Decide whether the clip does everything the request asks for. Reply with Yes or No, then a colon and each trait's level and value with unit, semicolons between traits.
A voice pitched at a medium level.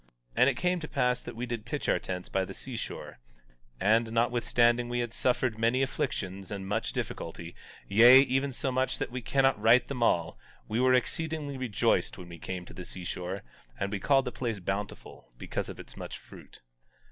No: low, 120 Hz